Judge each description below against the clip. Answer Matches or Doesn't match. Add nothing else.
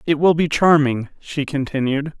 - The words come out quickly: Doesn't match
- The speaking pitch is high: Doesn't match